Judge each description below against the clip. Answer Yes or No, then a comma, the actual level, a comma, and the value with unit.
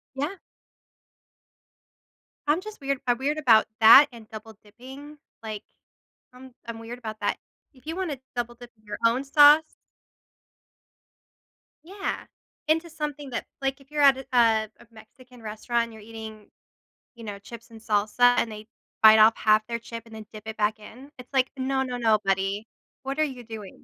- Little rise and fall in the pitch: No, average, 3.8 semitones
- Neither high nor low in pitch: No, high, 240 Hz